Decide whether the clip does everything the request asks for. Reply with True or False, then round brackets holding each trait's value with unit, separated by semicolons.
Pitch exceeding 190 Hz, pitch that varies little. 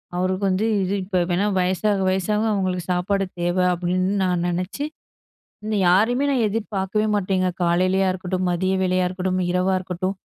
False (185 Hz; 1.7 semitones)